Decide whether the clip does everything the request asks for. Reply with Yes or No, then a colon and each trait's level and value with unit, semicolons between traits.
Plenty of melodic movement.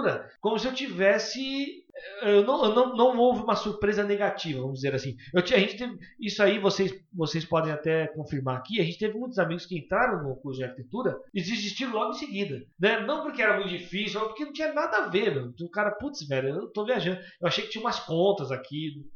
Yes: wide, 6.6 semitones